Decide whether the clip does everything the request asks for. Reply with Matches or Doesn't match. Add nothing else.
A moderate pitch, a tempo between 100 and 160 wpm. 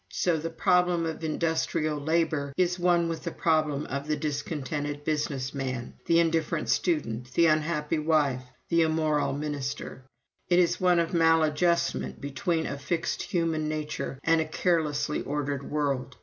Matches